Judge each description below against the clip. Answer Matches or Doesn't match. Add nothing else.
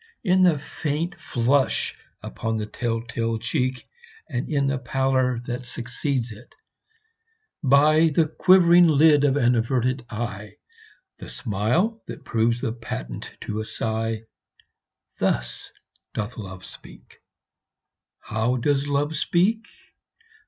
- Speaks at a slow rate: Matches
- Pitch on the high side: Doesn't match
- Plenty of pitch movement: Doesn't match